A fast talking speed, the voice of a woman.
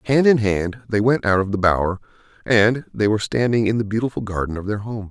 No: fast, 235 wpm; male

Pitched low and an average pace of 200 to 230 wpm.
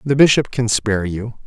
Yes: low, 115 Hz; fast, 205 wpm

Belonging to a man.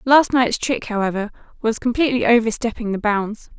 No: female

